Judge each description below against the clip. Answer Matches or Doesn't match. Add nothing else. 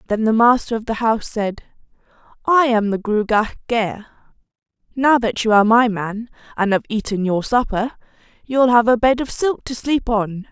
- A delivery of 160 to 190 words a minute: Matches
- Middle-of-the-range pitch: Doesn't match